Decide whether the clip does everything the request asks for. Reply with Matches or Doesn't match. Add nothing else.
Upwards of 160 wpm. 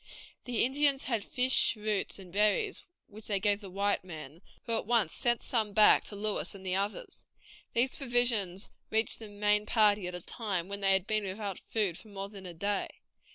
Matches